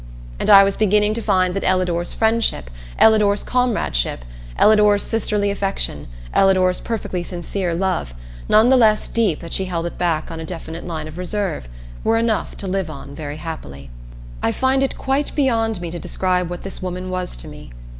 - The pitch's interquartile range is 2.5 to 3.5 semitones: No, average, 4.0 semitones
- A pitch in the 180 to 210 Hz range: Yes, medium, 185 Hz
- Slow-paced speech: No, average, 180 wpm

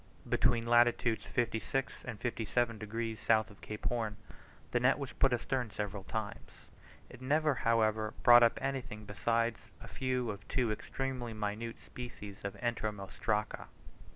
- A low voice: Yes, low, 115 Hz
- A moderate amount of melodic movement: No, narrow, 2.3 semitones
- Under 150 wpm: Yes, average, 140 wpm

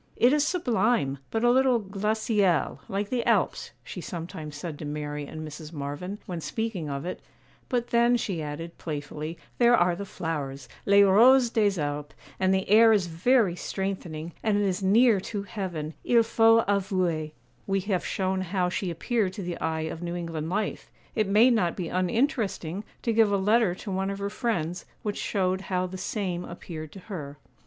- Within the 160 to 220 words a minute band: Yes, average, 180 wpm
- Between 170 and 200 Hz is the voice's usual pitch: Yes, high, 190 Hz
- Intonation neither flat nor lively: Yes, average, 4.7 semitones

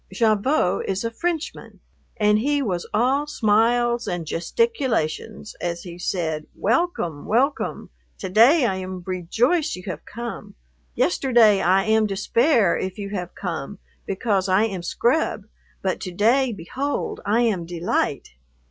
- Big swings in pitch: No, average, 4.7 semitones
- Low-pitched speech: No, high, 210 Hz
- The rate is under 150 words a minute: Yes, average, 140 wpm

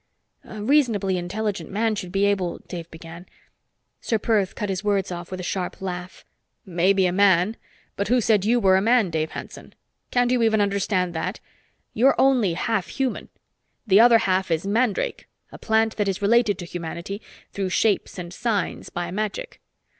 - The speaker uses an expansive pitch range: No, average, 3.5 semitones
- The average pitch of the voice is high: Yes, high, 200 Hz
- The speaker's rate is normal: Yes, average, 175 wpm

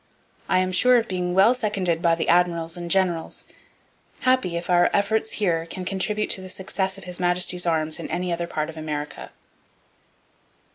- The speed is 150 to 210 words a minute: Yes, average, 180 wpm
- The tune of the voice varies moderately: No, narrow, 2.2 semitones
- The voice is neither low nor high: Yes, medium, 180 Hz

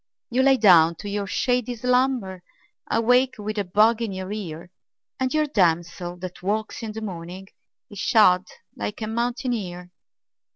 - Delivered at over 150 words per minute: Yes, average, 160 wpm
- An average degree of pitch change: Yes, average, 4.8 semitones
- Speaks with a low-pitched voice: No, high, 210 Hz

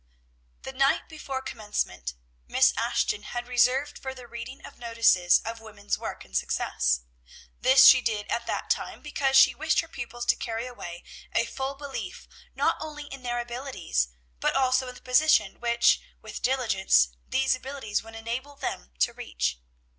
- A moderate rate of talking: Yes, average, 170 wpm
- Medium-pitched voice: No, high, 245 Hz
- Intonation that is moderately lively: Yes, average, 3.3 semitones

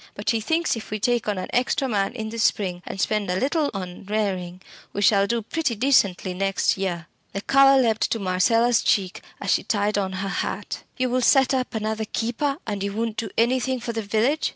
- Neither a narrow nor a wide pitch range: Yes, average, 3.9 semitones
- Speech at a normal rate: No, fast, 215 wpm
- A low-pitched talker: No, high, 220 Hz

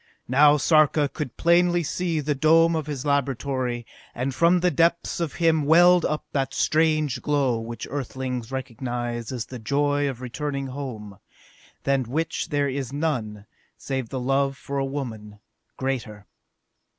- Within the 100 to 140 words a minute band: No, average, 150 wpm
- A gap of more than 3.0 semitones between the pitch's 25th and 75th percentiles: Yes, average, 3.4 semitones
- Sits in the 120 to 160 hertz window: Yes, medium, 140 Hz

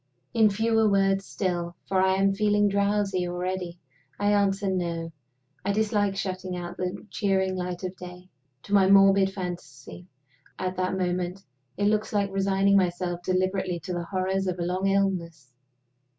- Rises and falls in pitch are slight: Yes, narrow, 1.7 semitones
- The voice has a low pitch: No, high, 190 Hz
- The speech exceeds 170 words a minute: No, average, 155 wpm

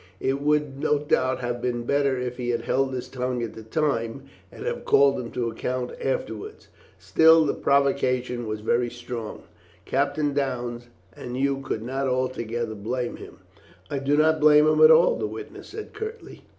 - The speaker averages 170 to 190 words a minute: Yes, average, 175 wpm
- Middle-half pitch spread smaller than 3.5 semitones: Yes, average, 2.9 semitones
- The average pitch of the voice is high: No, low, 130 Hz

